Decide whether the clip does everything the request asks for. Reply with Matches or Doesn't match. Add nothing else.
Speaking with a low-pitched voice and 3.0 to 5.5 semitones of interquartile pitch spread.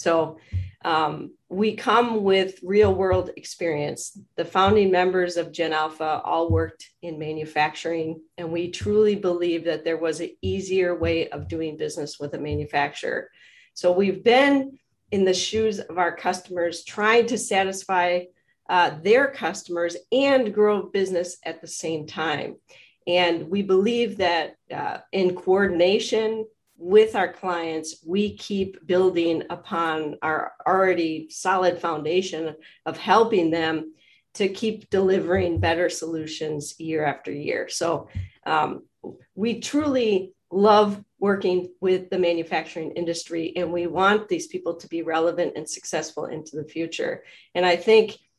Doesn't match